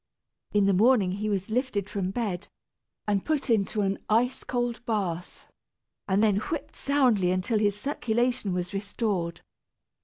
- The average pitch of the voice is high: Yes, high, 210 Hz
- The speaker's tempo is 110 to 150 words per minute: Yes, average, 145 wpm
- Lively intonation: No, average, 3.7 semitones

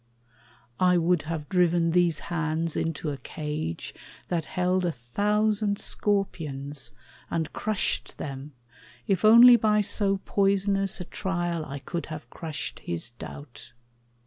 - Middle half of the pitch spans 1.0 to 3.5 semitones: No, average, 4.4 semitones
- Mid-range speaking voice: Yes, medium, 175 Hz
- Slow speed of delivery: Yes, slow, 125 wpm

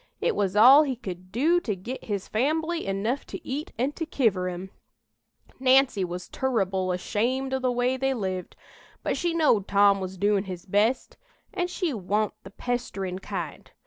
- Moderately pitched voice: No, high, 220 Hz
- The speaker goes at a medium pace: Yes, average, 175 wpm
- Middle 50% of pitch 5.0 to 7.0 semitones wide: Yes, wide, 5.6 semitones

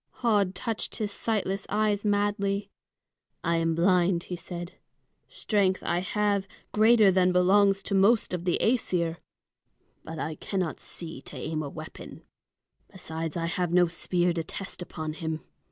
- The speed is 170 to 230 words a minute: No, average, 150 wpm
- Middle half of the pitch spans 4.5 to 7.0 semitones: No, average, 3.3 semitones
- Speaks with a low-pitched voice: No, medium, 185 Hz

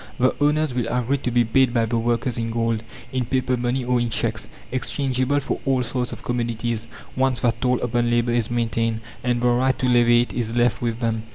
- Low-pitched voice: Yes, low, 120 Hz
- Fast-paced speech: Yes, fast, 215 wpm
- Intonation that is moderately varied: No, narrow, 1.5 semitones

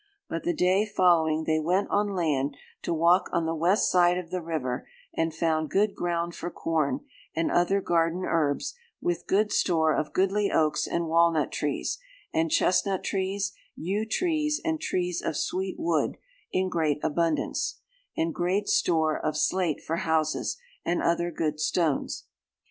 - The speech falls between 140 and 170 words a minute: Yes, average, 160 wpm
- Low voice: No, medium, 170 Hz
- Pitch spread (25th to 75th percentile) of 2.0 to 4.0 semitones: Yes, average, 2.8 semitones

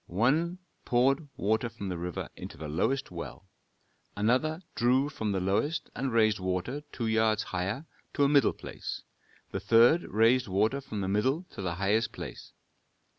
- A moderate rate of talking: Yes, average, 165 wpm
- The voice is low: Yes, low, 110 Hz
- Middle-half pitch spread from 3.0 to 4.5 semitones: No, wide, 5.6 semitones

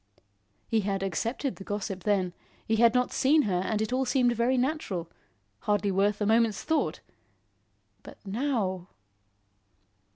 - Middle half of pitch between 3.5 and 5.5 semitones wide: Yes, average, 4.3 semitones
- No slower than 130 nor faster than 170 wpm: Yes, average, 140 wpm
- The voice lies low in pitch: No, high, 215 Hz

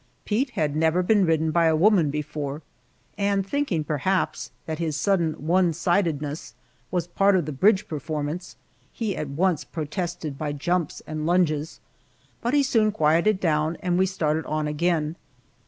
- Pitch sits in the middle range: Yes, medium, 165 Hz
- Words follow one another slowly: No, average, 155 wpm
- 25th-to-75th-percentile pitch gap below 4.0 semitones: Yes, average, 3.6 semitones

